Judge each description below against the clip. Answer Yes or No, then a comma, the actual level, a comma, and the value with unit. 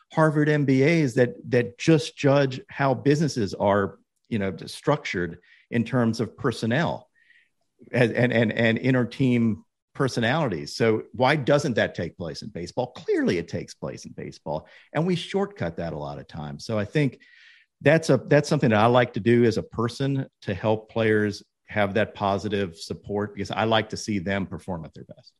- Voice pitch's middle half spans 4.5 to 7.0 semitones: Yes, average, 5.1 semitones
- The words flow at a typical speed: Yes, average, 180 wpm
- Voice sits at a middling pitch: No, low, 120 Hz